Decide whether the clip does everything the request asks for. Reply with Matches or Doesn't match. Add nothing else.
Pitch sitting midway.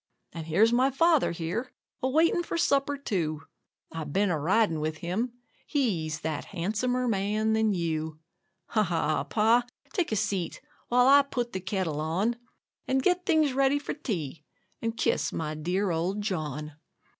Doesn't match